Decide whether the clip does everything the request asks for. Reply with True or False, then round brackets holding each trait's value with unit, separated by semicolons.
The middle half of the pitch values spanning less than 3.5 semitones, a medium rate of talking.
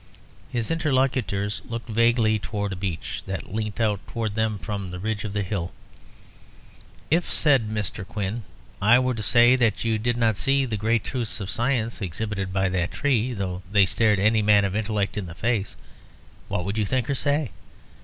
True (3.1 semitones; 185 wpm)